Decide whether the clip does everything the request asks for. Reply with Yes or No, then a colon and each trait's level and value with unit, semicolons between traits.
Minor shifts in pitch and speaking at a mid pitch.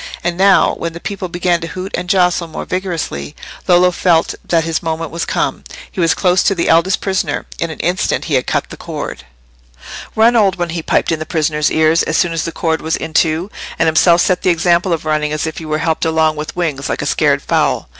Yes: narrow, 2.1 semitones; medium, 170 Hz